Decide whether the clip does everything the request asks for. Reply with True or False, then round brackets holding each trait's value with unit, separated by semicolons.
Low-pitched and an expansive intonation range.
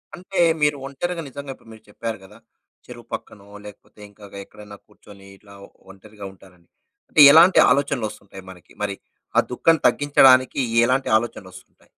True (110 Hz; 6.0 semitones)